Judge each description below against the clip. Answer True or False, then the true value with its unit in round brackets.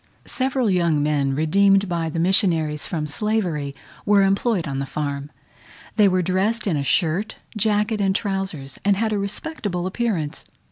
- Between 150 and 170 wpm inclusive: True (155 wpm)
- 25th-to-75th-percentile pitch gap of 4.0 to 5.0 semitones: False (5.4 semitones)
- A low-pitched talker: False (185 Hz)